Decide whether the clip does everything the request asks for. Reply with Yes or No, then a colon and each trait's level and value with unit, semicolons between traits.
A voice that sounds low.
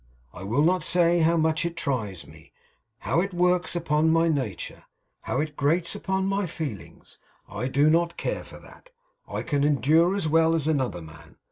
No: medium, 160 Hz